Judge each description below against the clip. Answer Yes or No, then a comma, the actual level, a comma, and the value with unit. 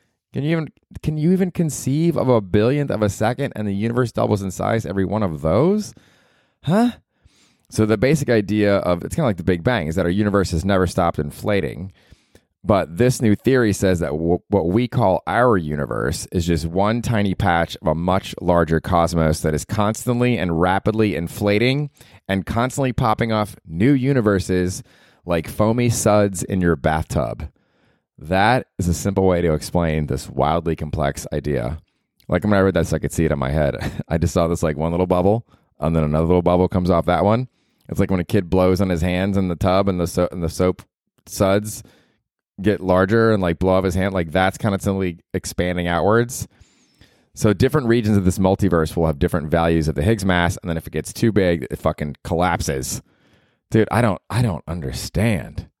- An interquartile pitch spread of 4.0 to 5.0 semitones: Yes, average, 4.4 semitones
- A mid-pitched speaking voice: No, very low, 95 Hz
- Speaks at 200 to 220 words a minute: Yes, fast, 205 wpm